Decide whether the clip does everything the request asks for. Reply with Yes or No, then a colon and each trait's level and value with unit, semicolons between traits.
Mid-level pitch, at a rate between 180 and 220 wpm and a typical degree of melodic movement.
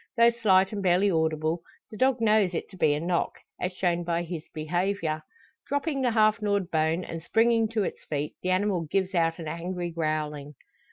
Yes: medium, 180 Hz; average, 190 wpm; average, 4.4 semitones